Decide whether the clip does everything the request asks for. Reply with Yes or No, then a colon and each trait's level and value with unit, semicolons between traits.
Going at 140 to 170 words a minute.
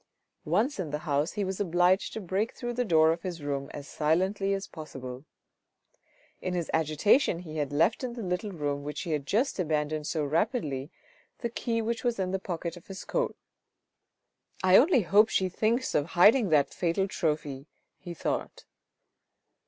No: average, 180 wpm